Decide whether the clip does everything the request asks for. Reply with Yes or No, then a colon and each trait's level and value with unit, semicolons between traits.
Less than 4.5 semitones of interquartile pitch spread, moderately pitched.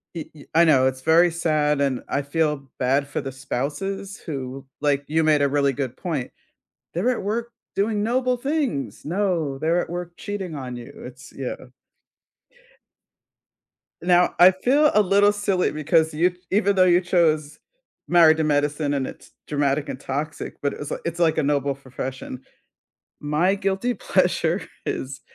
No: average, 4.8 semitones; medium, 160 Hz